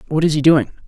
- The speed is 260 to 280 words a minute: Yes, fast, 275 wpm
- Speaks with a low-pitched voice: No, medium, 150 Hz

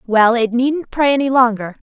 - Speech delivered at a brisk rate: No, average, 195 wpm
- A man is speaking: No, female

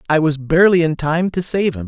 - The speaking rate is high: Yes, fast, 255 wpm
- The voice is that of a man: Yes, male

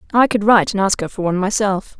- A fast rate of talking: Yes, fast, 270 wpm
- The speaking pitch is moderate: No, high, 200 Hz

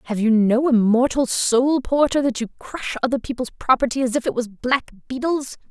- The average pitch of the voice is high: Yes, very high, 250 Hz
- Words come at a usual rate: Yes, average, 180 wpm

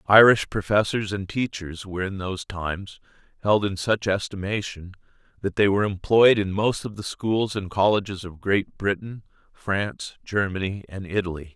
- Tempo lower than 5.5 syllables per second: Yes, 5.0 syllables/s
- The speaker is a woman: No, male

